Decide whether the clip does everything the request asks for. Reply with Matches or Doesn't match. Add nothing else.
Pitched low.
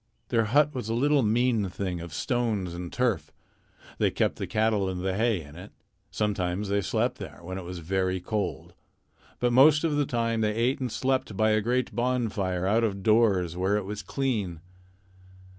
Matches